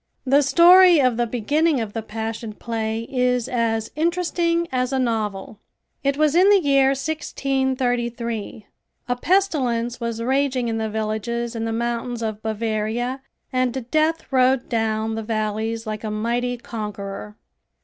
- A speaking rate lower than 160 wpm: Yes, average, 145 wpm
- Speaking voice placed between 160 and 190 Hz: No, high, 235 Hz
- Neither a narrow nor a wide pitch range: Yes, average, 3.3 semitones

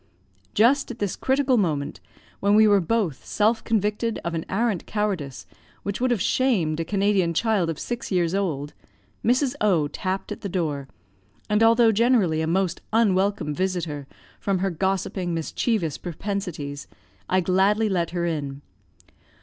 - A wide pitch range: No, average, 4.7 semitones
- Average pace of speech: Yes, average, 150 wpm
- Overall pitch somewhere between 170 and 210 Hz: Yes, high, 190 Hz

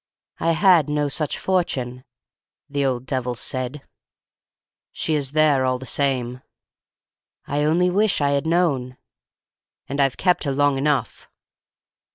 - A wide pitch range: No, average, 3.2 semitones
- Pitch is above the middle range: No, medium, 140 Hz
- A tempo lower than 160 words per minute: Yes, slow, 135 wpm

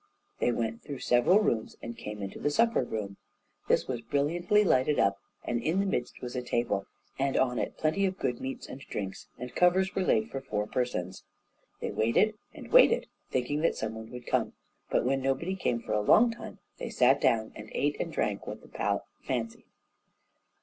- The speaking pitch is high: No, low, 125 Hz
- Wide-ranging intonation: Yes, wide, 6.8 semitones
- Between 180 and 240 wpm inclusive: Yes, average, 200 wpm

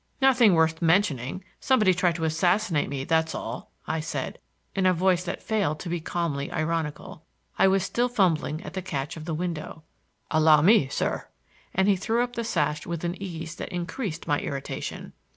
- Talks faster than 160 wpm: Yes, average, 180 wpm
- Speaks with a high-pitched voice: No, medium, 170 Hz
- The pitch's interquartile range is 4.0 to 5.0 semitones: No, average, 3.6 semitones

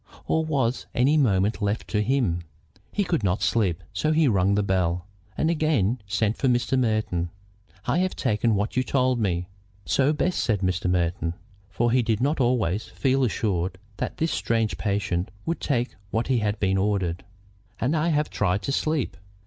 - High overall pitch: No, low, 110 Hz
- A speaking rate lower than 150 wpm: No, average, 175 wpm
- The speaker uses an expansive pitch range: Yes, wide, 5.7 semitones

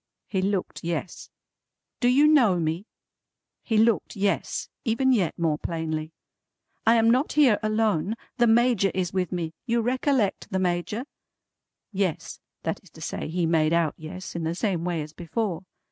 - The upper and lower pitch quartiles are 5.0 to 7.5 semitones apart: Yes, wide, 5.4 semitones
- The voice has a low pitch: No, high, 190 Hz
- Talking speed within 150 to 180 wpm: Yes, average, 160 wpm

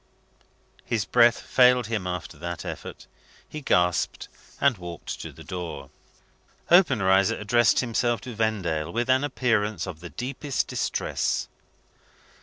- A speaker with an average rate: No, slow, 125 wpm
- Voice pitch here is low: Yes, low, 110 Hz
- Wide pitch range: Yes, wide, 5.7 semitones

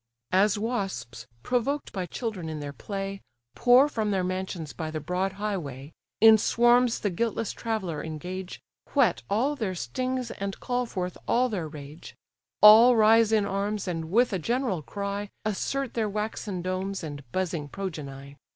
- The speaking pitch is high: Yes, high, 195 Hz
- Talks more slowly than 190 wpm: Yes, average, 155 wpm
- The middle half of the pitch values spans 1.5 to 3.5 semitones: No, average, 4.8 semitones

